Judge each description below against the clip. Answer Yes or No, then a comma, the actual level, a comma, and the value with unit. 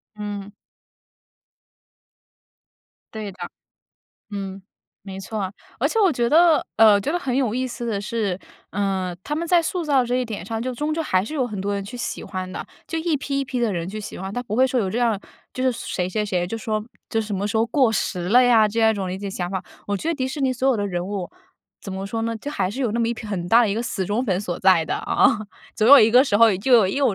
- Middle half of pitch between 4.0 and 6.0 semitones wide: Yes, average, 4.3 semitones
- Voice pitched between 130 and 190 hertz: No, high, 220 Hz